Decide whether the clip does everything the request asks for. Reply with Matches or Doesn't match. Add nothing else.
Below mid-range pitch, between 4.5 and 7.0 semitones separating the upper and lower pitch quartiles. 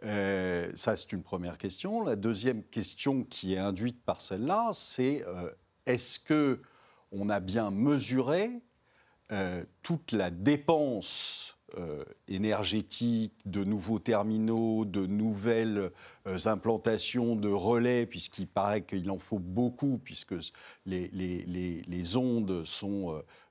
Doesn't match